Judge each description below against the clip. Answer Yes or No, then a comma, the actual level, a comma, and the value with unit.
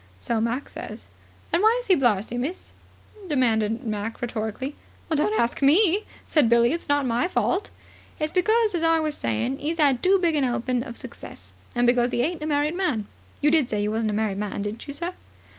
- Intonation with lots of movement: Yes, wide, 6.3 semitones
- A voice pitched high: Yes, very high, 260 Hz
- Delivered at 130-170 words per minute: No, fast, 205 wpm